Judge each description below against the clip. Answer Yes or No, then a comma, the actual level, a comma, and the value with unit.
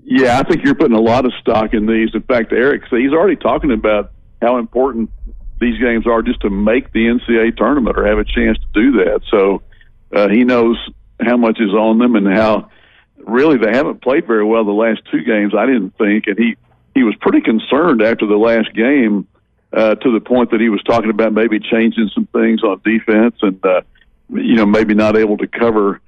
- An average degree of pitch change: No, narrow, 1.5 semitones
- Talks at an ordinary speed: No, fast, 215 wpm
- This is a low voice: Yes, low, 110 Hz